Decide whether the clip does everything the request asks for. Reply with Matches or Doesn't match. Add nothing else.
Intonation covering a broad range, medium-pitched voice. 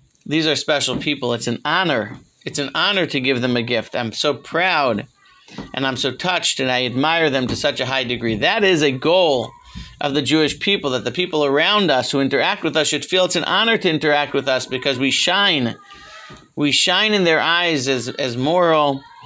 Doesn't match